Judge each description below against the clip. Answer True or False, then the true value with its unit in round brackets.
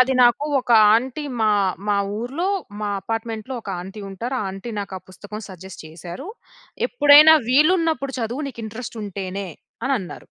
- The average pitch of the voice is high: True (230 Hz)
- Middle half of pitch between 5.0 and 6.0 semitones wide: True (5.5 semitones)